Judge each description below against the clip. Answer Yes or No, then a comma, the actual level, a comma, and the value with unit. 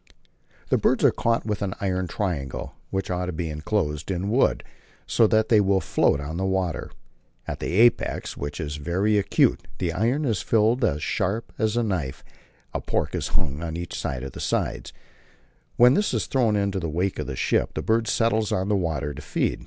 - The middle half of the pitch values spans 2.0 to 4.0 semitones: No, wide, 5.4 semitones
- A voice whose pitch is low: Yes, very low, 95 Hz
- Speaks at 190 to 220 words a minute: Yes, average, 200 wpm